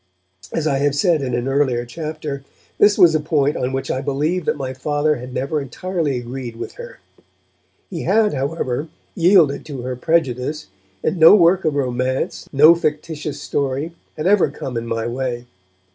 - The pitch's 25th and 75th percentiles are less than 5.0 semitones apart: Yes, average, 3.9 semitones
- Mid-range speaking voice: Yes, medium, 145 Hz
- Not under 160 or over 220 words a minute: Yes, average, 175 wpm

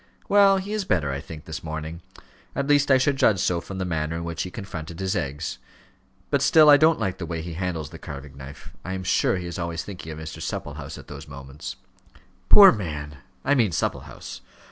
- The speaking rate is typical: No, fast, 215 wpm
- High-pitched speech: No, very low, 85 Hz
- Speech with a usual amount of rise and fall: No, wide, 7.5 semitones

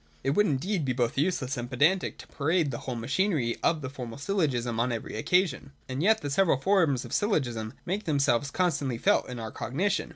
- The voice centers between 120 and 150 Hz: Yes, medium, 140 Hz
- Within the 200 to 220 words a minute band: Yes, fast, 205 wpm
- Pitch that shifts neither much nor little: No, wide, 6.7 semitones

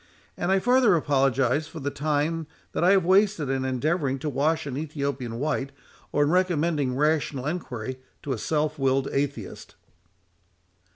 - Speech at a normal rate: Yes, average, 155 wpm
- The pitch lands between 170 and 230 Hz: No, medium, 145 Hz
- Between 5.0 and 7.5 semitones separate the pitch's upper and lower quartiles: No, average, 3.3 semitones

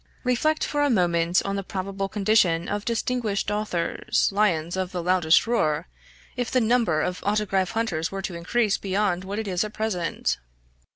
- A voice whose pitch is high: Yes, high, 195 Hz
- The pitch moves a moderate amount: Yes, average, 3.6 semitones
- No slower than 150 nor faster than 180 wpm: Yes, average, 170 wpm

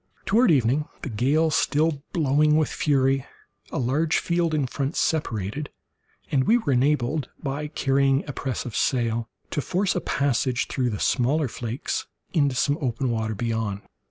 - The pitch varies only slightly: No, average, 3.8 semitones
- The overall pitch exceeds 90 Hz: Yes, low, 135 Hz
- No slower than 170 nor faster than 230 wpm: No, average, 155 wpm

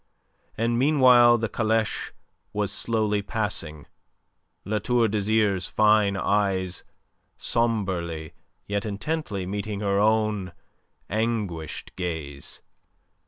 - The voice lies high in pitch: No, low, 105 Hz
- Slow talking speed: Yes, slow, 90 wpm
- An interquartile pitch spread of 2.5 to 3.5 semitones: Yes, average, 2.8 semitones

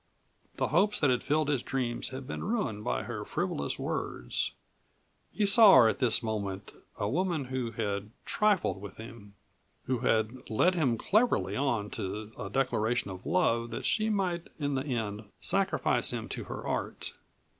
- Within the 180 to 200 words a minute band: No, average, 165 wpm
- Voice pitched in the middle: No, low, 125 Hz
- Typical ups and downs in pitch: No, wide, 6.6 semitones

